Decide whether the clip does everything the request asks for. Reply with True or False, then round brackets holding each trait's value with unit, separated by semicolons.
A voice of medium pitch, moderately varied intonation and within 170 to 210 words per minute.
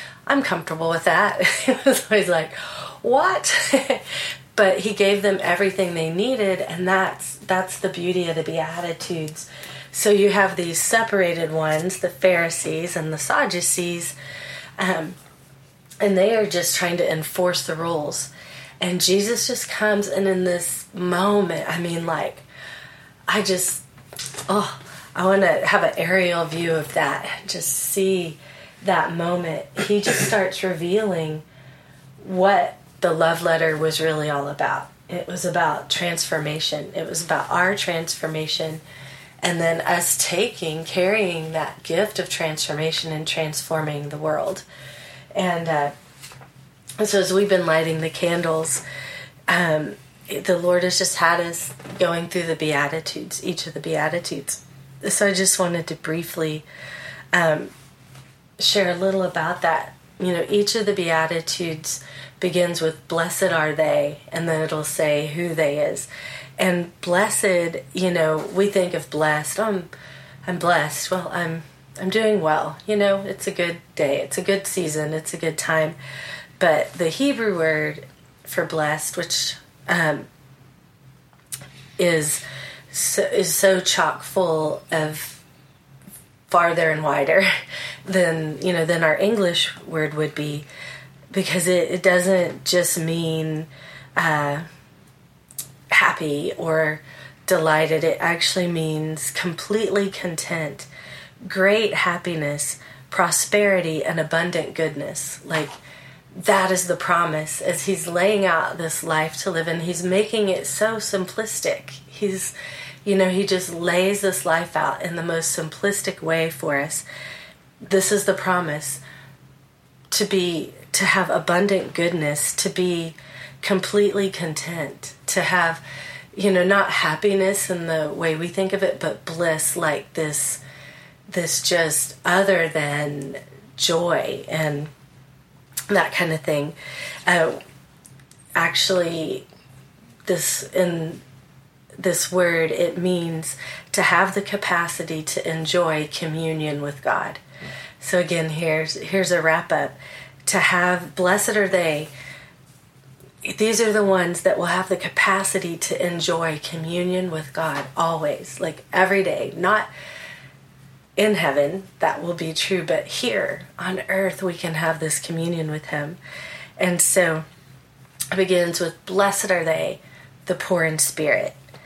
False (165 Hz; 3.3 semitones; 135 wpm)